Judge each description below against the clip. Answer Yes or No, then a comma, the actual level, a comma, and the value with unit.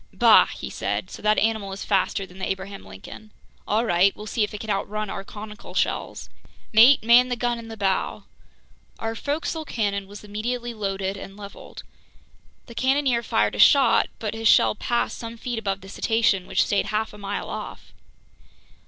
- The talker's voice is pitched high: Yes, high, 215 Hz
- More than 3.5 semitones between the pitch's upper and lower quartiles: No, average, 2.9 semitones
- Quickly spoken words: No, average, 185 wpm